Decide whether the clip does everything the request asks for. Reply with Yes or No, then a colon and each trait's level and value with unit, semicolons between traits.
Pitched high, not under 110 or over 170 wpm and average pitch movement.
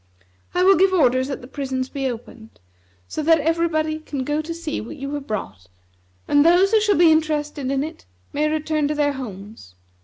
No: very high, 295 Hz; average, 195 wpm; average, 3.4 semitones